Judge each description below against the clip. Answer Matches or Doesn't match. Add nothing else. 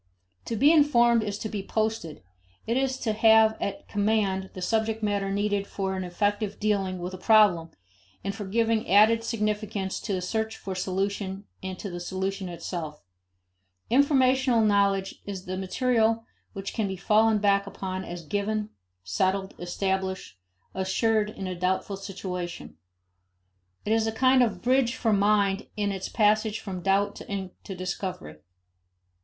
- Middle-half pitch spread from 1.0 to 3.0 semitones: Matches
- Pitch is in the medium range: Doesn't match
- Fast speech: Doesn't match